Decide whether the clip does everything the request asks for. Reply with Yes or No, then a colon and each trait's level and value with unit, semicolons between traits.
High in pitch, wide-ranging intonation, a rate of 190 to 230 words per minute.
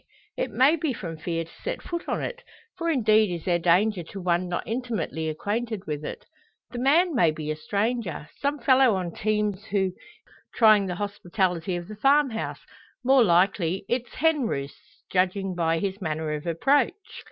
No: high, 200 Hz; wide, 6.1 semitones; average, 175 wpm